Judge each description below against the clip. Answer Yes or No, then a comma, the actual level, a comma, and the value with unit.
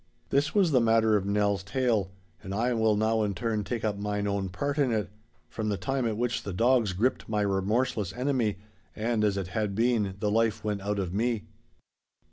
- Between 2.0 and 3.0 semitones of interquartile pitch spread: Yes, average, 2.7 semitones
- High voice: No, low, 110 Hz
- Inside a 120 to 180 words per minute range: No, fast, 205 wpm